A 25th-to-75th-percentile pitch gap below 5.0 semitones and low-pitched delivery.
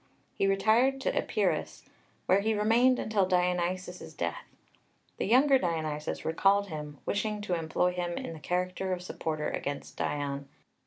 No: average, 4.5 semitones; medium, 180 Hz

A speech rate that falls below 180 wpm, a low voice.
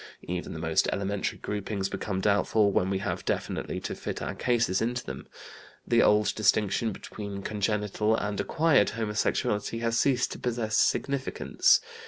Yes: average, 150 wpm; low, 105 Hz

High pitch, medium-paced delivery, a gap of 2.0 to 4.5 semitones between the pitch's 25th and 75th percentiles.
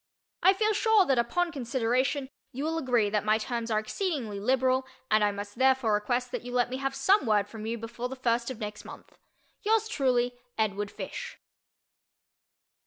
Yes: high, 245 Hz; average, 180 wpm; average, 3.8 semitones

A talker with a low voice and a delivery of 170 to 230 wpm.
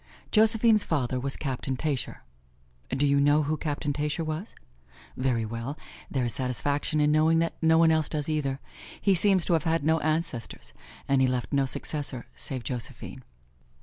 No: medium, 150 Hz; average, 175 wpm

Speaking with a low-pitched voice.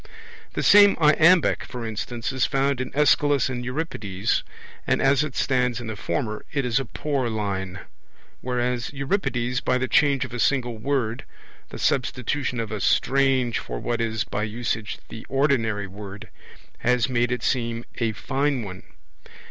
Yes: low, 125 Hz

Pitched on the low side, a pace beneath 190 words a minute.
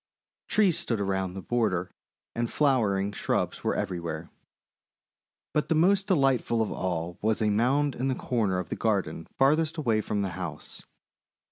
Yes: low, 110 Hz; average, 160 wpm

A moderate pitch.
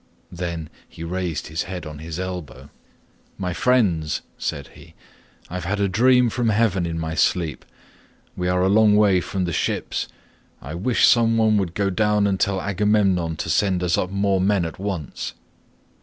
No: very low, 95 Hz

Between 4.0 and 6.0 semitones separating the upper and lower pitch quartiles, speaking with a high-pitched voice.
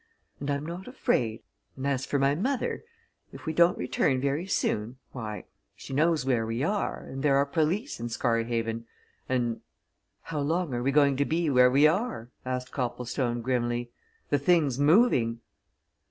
No: average, 4.5 semitones; low, 135 Hz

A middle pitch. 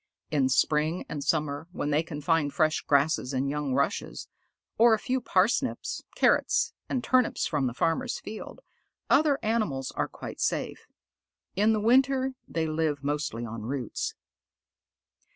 Yes: medium, 155 Hz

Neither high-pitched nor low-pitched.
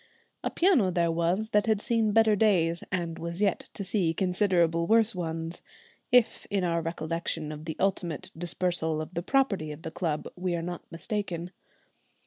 Yes: medium, 175 Hz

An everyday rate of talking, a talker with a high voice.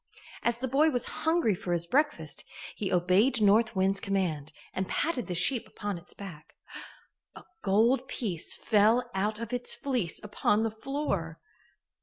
Yes: average, 155 wpm; high, 210 Hz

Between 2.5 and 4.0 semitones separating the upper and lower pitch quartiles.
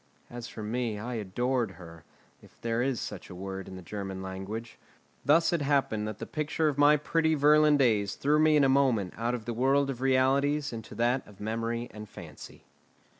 No: average, 4.9 semitones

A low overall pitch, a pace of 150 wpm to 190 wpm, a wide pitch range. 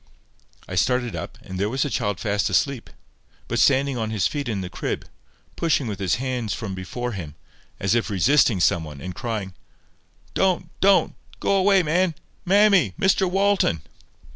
Yes: low, 120 Hz; average, 165 wpm; wide, 8.5 semitones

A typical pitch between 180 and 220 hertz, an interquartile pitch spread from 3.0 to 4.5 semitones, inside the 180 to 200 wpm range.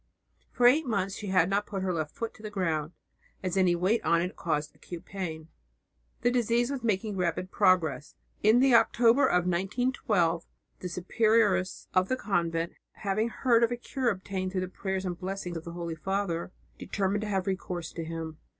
Yes: high, 190 Hz; average, 4.0 semitones; average, 185 wpm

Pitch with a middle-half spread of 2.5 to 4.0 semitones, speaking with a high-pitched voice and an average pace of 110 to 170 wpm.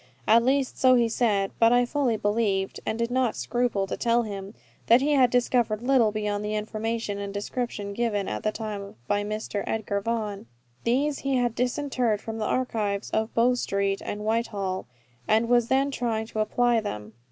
No: average, 3.0 semitones; high, 225 Hz; average, 185 wpm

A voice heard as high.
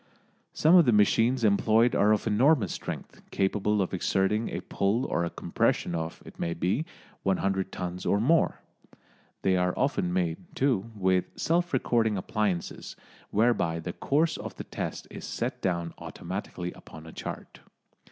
No: low, 100 Hz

